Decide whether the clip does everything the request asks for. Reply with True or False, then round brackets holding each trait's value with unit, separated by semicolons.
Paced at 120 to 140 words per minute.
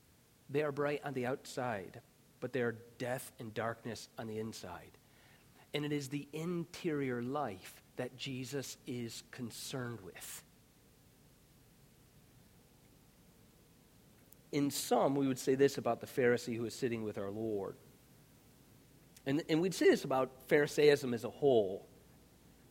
True (135 wpm)